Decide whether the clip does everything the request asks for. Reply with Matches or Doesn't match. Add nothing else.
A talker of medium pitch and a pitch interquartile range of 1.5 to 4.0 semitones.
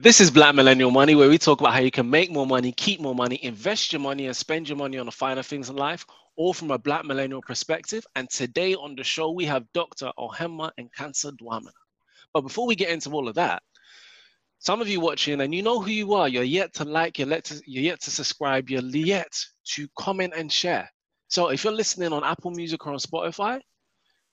Doesn't match